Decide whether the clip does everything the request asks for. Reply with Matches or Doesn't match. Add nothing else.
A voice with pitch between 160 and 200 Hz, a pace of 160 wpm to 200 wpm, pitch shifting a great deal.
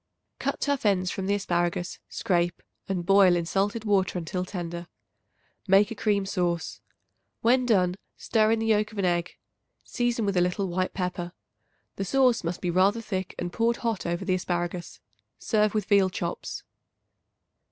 Doesn't match